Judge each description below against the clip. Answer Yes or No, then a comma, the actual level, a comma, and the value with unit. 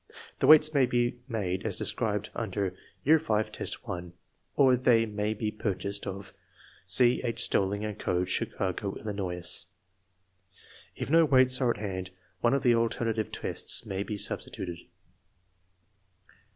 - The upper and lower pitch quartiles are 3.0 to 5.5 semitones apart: Yes, average, 4.0 semitones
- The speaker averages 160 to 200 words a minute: No, average, 140 wpm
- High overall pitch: No, low, 105 Hz